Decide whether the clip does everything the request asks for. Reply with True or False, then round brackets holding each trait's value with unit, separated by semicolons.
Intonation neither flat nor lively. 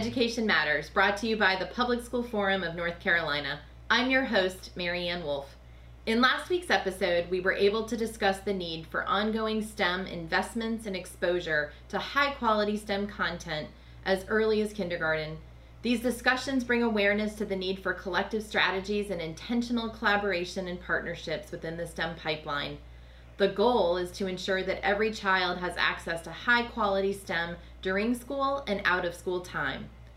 True (4.1 semitones)